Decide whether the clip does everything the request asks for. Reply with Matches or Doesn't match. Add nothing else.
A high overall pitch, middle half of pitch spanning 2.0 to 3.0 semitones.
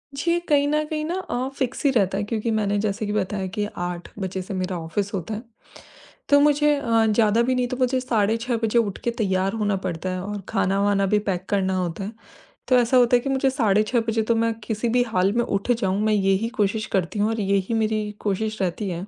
Doesn't match